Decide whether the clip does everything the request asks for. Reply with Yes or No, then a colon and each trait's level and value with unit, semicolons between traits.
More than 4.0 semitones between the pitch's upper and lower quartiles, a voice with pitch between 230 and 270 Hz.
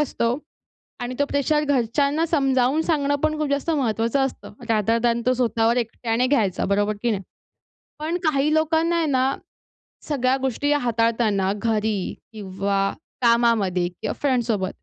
Yes: average, 4.5 semitones; high, 245 Hz